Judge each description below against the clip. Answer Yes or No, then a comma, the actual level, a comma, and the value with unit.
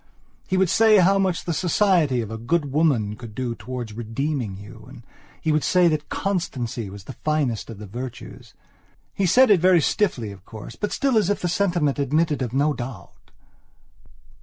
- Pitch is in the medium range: Yes, medium, 145 Hz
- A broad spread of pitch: Yes, wide, 7.4 semitones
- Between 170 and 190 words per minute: Yes, average, 185 wpm